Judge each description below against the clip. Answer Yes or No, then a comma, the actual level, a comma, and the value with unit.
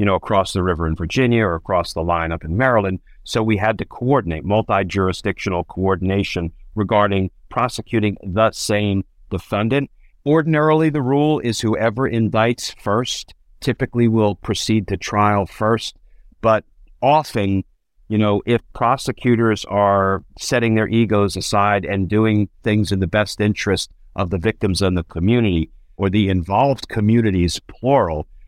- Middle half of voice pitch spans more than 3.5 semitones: No, average, 3.2 semitones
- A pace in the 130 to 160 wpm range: Yes, average, 145 wpm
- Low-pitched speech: Yes, low, 105 Hz